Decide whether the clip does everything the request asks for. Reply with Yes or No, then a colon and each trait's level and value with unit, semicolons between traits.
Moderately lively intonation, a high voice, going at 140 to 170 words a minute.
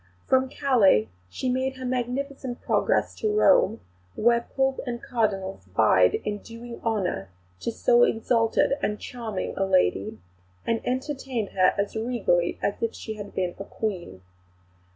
Yes: average, 4.8 semitones; high, 230 Hz; average, 145 wpm